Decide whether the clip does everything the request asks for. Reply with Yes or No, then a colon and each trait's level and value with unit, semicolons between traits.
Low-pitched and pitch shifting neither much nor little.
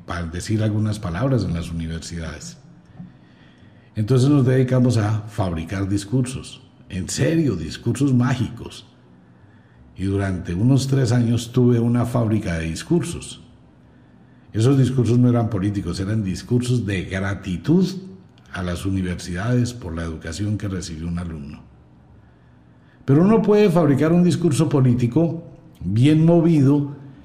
No: low, 110 Hz; wide, 7.0 semitones